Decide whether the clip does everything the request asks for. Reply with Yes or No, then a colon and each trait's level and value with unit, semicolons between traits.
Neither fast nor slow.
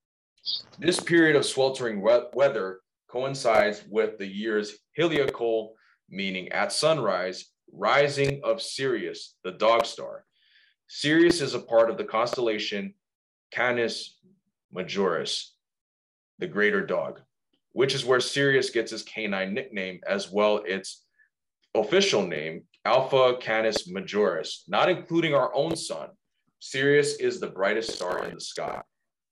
No: slow, 125 wpm